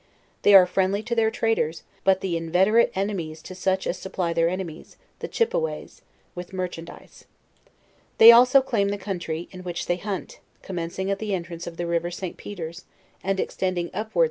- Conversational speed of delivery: Yes, average, 175 wpm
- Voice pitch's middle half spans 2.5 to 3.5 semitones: Yes, average, 2.9 semitones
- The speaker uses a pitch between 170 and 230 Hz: Yes, medium, 185 Hz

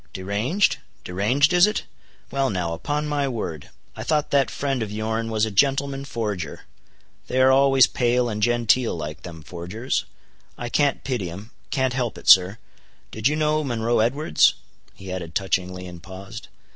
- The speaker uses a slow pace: No, average, 160 wpm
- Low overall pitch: Yes, low, 115 Hz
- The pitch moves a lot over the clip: Yes, wide, 6.3 semitones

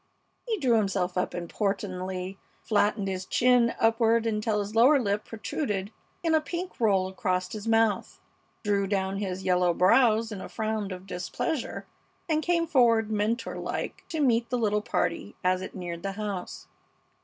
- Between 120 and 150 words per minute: No, average, 160 wpm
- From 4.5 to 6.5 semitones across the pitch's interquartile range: No, average, 3.6 semitones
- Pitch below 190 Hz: No, high, 210 Hz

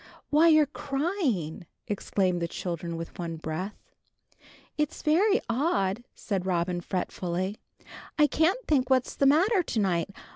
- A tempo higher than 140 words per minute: No, slow, 135 wpm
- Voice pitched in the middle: No, high, 210 Hz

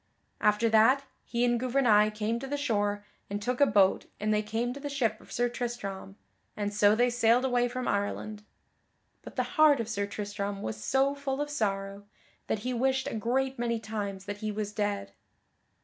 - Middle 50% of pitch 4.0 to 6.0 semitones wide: No, average, 3.4 semitones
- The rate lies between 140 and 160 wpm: No, average, 195 wpm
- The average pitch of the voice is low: No, high, 225 Hz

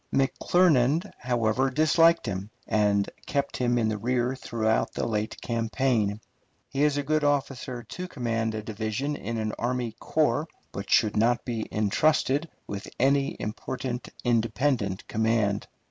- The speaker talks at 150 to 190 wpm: No, average, 140 wpm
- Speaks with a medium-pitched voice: No, low, 120 Hz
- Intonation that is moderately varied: Yes, average, 3.9 semitones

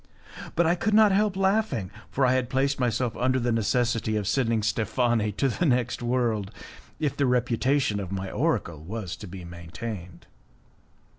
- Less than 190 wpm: Yes, average, 165 wpm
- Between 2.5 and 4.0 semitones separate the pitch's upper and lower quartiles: No, average, 4.5 semitones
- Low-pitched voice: Yes, low, 120 Hz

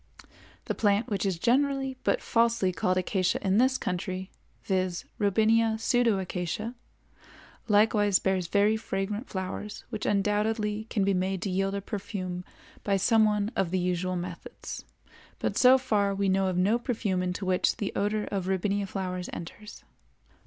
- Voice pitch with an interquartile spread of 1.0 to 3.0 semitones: Yes, narrow, 2.6 semitones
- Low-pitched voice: No, high, 200 Hz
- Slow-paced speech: No, average, 150 wpm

